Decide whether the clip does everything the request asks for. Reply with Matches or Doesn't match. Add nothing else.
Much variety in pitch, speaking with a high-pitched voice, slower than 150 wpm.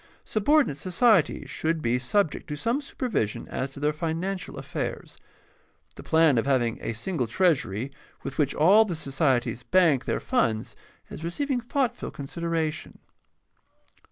Doesn't match